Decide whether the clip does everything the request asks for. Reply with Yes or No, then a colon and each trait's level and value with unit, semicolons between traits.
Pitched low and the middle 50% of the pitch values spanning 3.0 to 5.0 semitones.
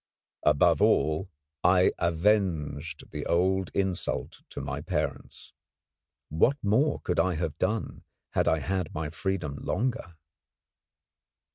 Yes: very low, 90 Hz; average, 3.8 semitones